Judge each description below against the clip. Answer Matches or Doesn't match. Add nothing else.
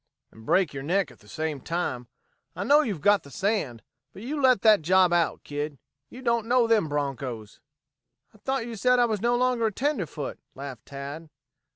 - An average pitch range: Doesn't match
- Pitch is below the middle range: Doesn't match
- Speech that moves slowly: Doesn't match